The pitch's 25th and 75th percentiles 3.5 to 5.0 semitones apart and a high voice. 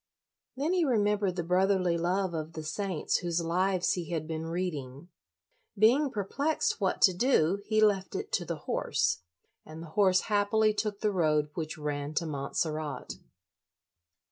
No: average, 4.5 semitones; medium, 180 Hz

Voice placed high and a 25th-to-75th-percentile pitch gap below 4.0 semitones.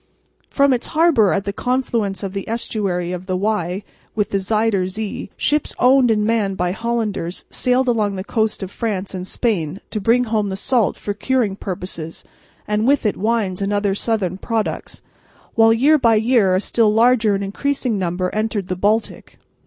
Yes: high, 210 Hz; average, 3.2 semitones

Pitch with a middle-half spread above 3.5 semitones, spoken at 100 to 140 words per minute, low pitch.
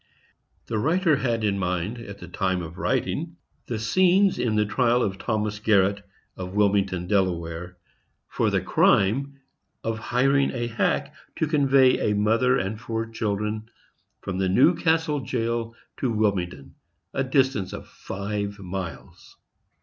Yes: average, 4.6 semitones; slow, 135 wpm; low, 110 Hz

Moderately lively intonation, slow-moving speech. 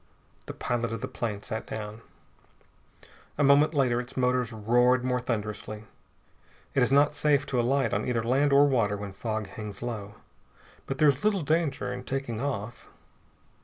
No: average, 4.0 semitones; average, 165 wpm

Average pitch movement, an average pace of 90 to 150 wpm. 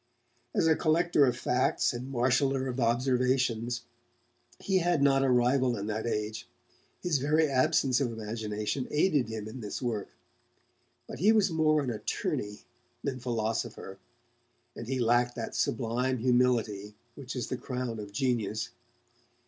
Yes: average, 3.2 semitones; average, 145 wpm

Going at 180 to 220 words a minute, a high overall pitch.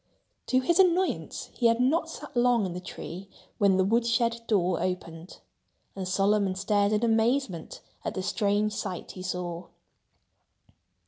No: average, 150 wpm; high, 205 Hz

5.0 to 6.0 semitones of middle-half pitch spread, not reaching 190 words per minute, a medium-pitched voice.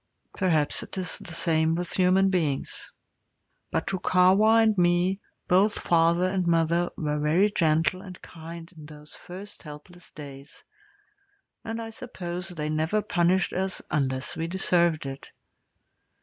No: average, 3.0 semitones; average, 140 wpm; medium, 175 Hz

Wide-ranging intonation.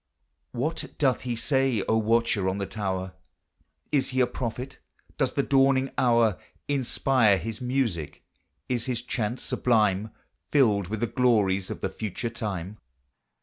No: average, 3.8 semitones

